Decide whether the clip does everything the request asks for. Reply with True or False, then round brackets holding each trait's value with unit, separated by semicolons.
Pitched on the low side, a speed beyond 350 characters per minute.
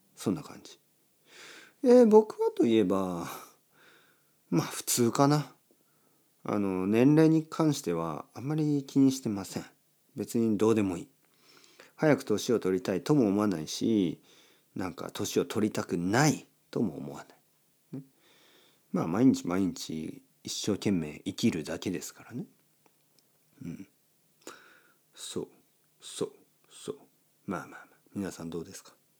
False (110 Hz; 250 characters per minute)